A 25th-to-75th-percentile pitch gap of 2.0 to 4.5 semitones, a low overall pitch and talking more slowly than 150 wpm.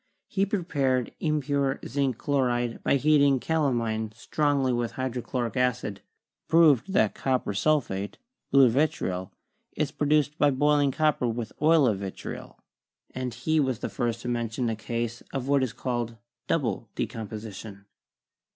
Yes: average, 3.8 semitones; low, 130 Hz; average, 140 wpm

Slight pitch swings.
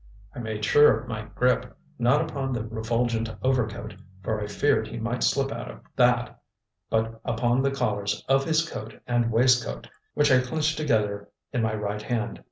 No: average, 3.1 semitones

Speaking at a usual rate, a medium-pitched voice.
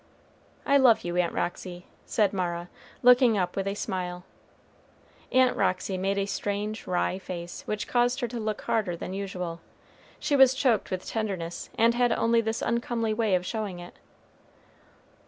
No: average, 160 wpm; high, 200 Hz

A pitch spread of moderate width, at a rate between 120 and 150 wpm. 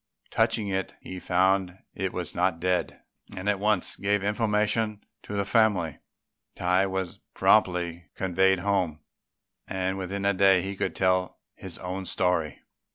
No: narrow, 1.8 semitones; average, 145 wpm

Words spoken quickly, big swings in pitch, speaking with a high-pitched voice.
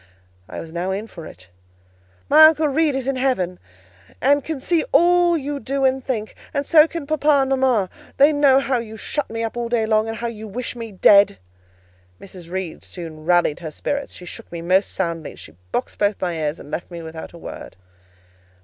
Yes: fast, 210 wpm; wide, 7.8 semitones; high, 230 Hz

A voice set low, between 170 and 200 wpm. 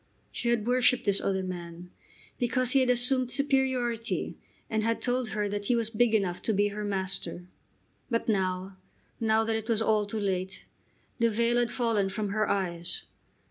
No: high, 220 Hz; average, 180 wpm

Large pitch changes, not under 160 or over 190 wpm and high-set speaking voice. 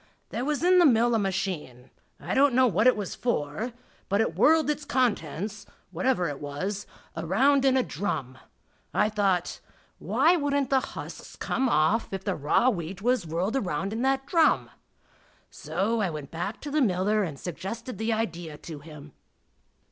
Yes: wide, 7.0 semitones; average, 170 wpm; high, 210 Hz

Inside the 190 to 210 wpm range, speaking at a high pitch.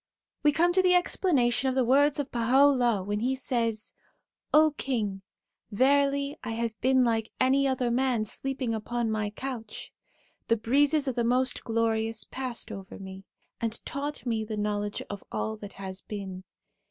No: average, 170 wpm; high, 240 Hz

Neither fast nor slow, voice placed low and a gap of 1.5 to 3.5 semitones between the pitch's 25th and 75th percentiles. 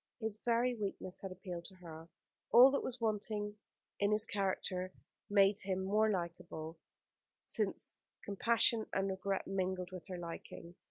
No: average, 145 wpm; high, 195 Hz; average, 2.8 semitones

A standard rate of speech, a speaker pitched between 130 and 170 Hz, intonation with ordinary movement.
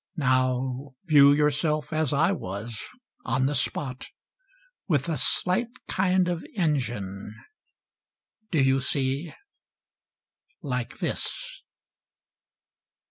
No: slow, 95 wpm; medium, 140 Hz; average, 4.2 semitones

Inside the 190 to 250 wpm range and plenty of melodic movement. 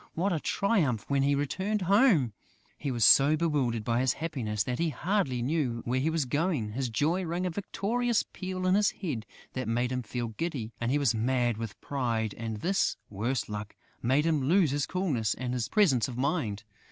Yes: average, 195 wpm; wide, 6.3 semitones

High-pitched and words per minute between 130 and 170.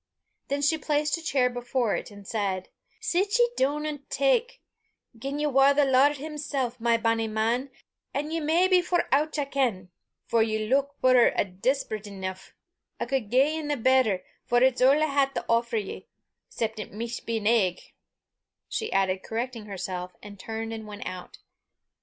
No: very high, 250 Hz; average, 180 wpm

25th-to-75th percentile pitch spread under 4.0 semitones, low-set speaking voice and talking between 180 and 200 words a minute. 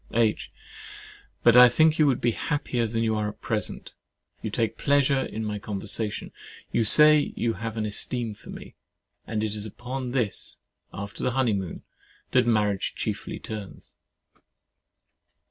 No: average, 2.9 semitones; low, 115 Hz; average, 155 wpm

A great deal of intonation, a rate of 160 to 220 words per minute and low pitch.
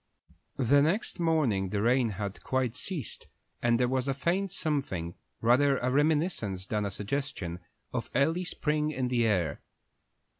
No: wide, 6.1 semitones; average, 150 wpm; low, 130 Hz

